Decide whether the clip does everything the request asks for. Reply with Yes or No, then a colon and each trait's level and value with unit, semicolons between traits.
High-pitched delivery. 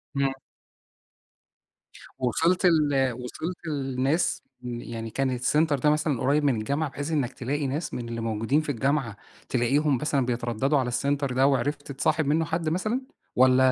No: medium, 140 Hz